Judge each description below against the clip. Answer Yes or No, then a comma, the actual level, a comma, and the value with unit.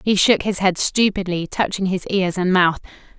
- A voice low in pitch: No, medium, 185 Hz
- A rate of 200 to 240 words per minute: No, average, 190 wpm